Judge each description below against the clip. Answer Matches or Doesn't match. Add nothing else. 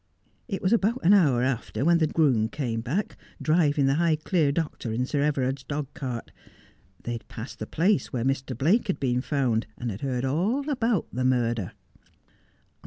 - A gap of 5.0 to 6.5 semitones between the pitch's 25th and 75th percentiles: Matches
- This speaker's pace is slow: Doesn't match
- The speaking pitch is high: Doesn't match